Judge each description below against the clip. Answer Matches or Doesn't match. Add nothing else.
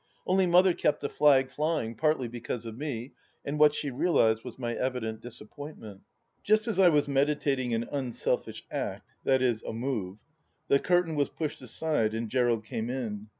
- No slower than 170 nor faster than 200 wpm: Matches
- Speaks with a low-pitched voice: Matches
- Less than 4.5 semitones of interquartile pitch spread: Doesn't match